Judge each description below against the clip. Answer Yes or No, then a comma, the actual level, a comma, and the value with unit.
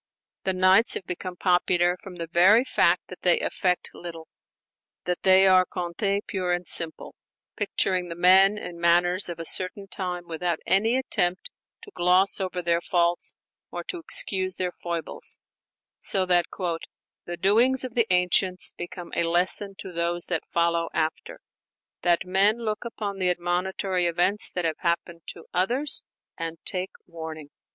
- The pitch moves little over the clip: Yes, narrow, 1.9 semitones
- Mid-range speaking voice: Yes, medium, 180 Hz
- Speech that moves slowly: No, average, 160 wpm